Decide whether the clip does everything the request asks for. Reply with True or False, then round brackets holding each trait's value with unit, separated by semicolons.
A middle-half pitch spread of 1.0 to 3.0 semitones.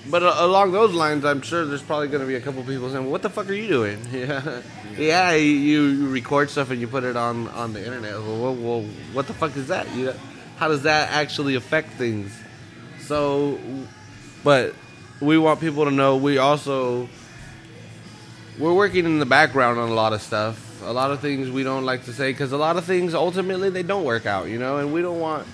False (4.2 semitones)